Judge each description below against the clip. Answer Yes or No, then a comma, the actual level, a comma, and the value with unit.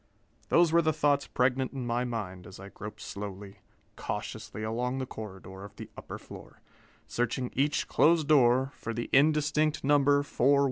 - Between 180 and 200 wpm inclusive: No, average, 160 wpm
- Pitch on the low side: Yes, low, 125 Hz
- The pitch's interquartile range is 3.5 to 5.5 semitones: Yes, average, 4.8 semitones